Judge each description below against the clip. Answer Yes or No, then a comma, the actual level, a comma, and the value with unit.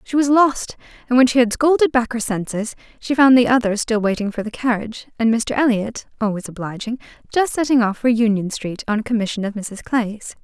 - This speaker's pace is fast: Yes, fast, 215 wpm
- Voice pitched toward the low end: No, high, 235 Hz